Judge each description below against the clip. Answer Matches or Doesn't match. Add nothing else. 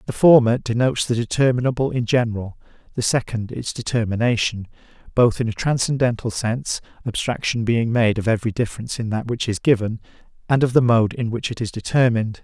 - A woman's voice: Doesn't match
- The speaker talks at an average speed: Matches